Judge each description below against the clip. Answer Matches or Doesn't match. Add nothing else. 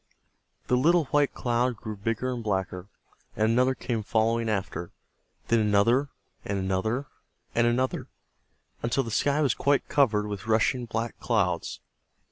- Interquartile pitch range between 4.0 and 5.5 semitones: Doesn't match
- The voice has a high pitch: Doesn't match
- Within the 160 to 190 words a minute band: Doesn't match